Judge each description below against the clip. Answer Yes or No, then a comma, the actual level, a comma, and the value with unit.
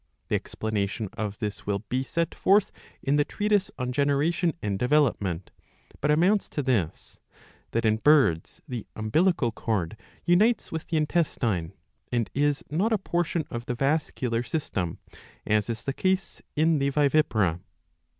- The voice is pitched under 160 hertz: Yes, low, 135 Hz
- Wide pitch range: Yes, wide, 6.7 semitones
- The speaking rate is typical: Yes, average, 150 wpm